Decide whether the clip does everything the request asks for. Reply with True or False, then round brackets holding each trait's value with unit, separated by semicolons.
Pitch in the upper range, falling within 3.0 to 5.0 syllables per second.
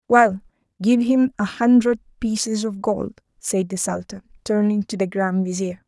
True (210 Hz; 4.5 syllables/s)